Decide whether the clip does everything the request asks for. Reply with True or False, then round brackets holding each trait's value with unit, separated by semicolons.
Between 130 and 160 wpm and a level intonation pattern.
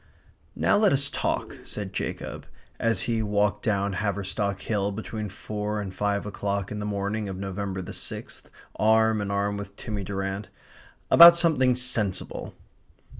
True (150 wpm; 1.8 semitones)